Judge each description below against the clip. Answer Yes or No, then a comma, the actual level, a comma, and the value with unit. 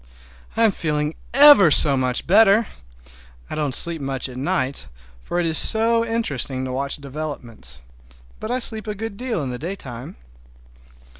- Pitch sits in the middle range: Yes, medium, 155 Hz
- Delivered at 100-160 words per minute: Yes, average, 155 wpm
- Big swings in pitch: Yes, wide, 8.7 semitones